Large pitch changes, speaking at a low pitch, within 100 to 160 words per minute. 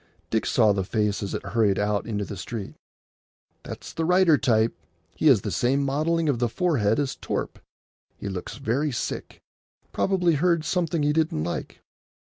No: wide, 7.2 semitones; low, 125 Hz; average, 170 wpm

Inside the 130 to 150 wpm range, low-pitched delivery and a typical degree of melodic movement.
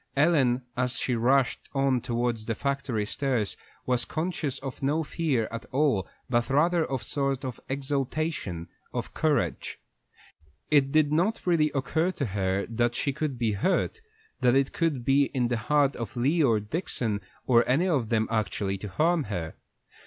No: average, 165 wpm; low, 130 Hz; average, 4.4 semitones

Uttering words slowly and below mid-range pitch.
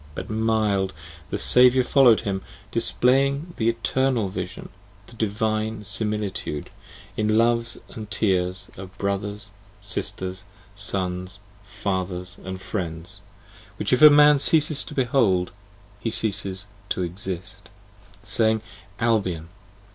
Yes: slow, 110 wpm; low, 105 Hz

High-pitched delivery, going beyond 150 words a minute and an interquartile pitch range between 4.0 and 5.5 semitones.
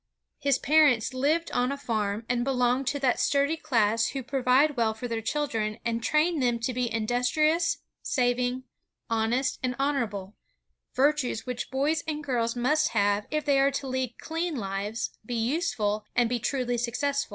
No: very high, 250 Hz; average, 170 wpm; average, 3.5 semitones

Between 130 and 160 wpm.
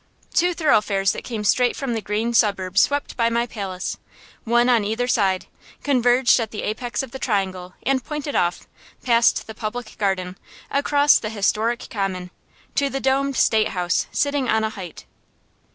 No: average, 170 wpm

